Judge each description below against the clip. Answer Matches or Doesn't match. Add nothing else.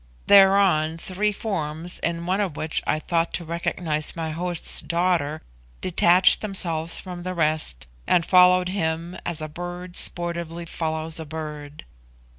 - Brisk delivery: Doesn't match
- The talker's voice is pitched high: Doesn't match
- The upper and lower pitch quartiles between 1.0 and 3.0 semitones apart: Matches